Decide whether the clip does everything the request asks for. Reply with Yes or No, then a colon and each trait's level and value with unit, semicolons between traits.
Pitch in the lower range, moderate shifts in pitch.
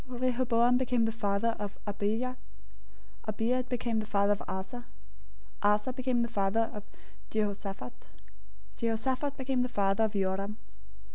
No: high, 225 Hz; average, 3.4 semitones